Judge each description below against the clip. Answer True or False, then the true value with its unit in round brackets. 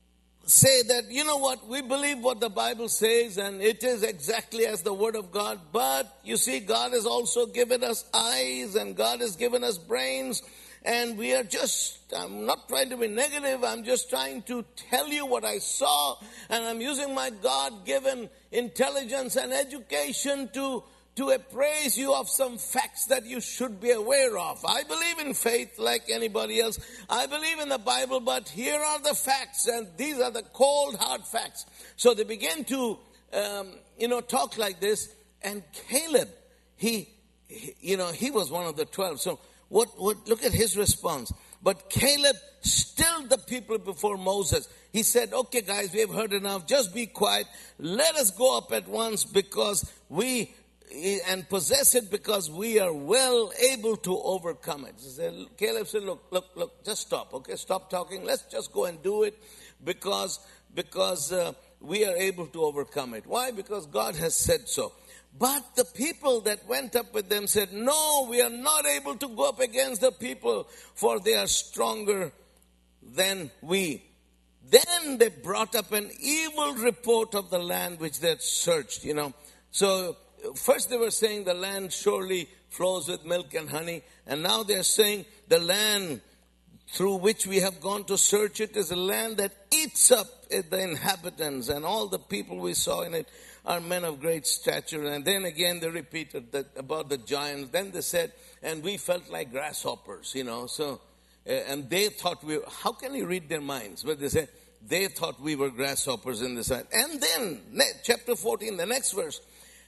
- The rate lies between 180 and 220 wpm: True (185 wpm)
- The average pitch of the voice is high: True (225 Hz)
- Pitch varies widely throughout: True (6.0 semitones)